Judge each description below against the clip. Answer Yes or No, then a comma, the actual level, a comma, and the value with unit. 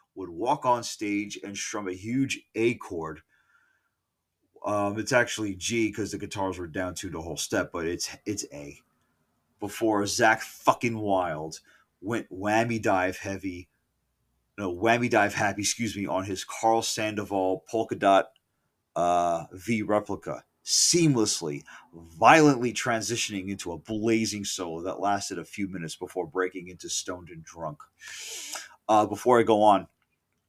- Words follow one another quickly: No, average, 145 wpm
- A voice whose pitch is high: No, low, 100 Hz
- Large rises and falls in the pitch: No, average, 3.3 semitones